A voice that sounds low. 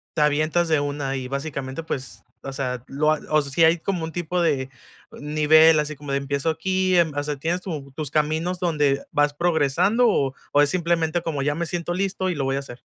No: medium, 155 Hz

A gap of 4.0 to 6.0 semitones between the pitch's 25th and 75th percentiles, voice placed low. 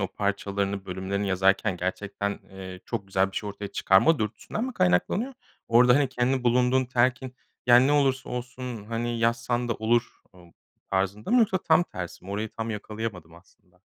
Yes: average, 4.5 semitones; low, 110 Hz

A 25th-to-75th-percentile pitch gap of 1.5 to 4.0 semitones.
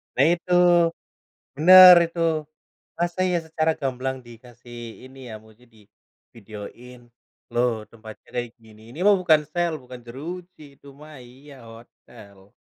No: average, 5.2 semitones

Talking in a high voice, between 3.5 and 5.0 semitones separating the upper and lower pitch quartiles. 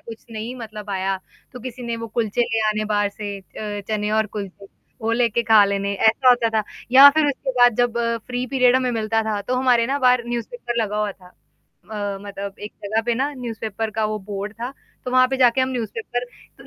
No: high, 225 Hz; average, 2.9 semitones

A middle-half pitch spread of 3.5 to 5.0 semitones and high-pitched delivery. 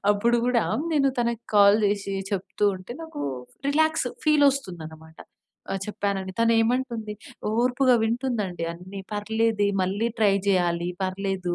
Yes: average, 4.0 semitones; high, 210 Hz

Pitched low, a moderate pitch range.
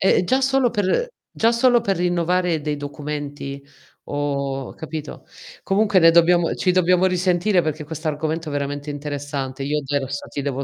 No: medium, 160 Hz; average, 4.2 semitones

